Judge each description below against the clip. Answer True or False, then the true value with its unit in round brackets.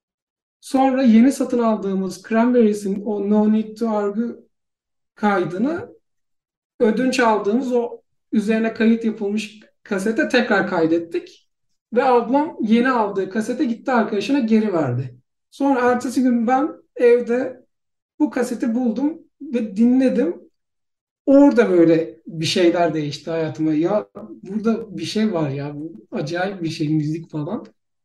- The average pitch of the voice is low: False (225 Hz)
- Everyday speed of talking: True (120 wpm)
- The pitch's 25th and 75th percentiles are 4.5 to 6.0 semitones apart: True (4.8 semitones)